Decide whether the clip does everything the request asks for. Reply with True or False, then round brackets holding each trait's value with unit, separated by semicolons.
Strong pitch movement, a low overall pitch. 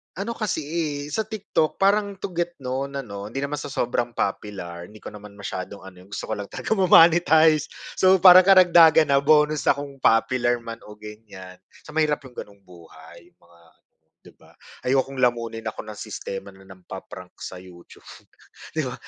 True (8.0 semitones; 125 Hz)